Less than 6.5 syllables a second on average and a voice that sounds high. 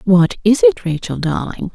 Yes: 4.6 syllables/s; high, 210 Hz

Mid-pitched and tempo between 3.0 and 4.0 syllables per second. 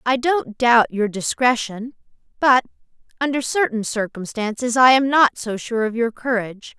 No: high, 240 Hz; 3.8 syllables/s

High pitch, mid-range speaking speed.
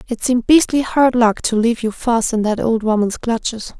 No: high, 230 Hz; fast, 220 wpm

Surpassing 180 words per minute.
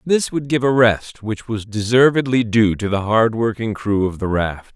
Yes: average, 200 wpm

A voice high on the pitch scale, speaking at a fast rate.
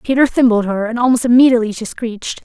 No: high, 235 Hz; average, 195 wpm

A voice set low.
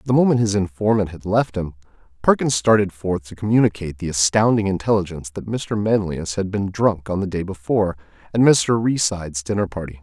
Yes: low, 100 Hz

